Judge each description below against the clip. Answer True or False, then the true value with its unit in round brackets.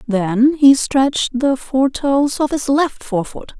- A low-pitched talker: False (265 Hz)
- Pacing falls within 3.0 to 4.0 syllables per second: True (3.8 syllables/s)